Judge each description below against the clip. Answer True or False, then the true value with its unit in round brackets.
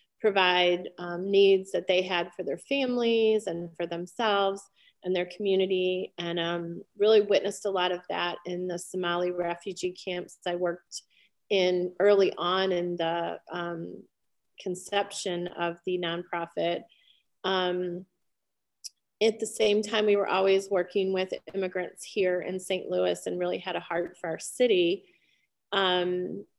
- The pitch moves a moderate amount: False (2.0 semitones)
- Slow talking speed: False (145 wpm)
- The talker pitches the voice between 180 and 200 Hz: True (185 Hz)